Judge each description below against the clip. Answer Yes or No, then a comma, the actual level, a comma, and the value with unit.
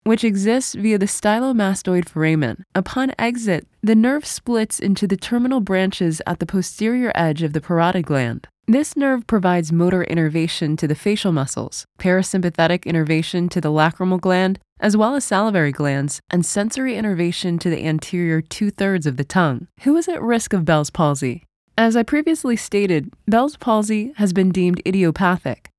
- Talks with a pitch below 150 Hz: No, medium, 185 Hz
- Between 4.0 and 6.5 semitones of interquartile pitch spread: Yes, average, 4.9 semitones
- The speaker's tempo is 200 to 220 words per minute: No, average, 165 wpm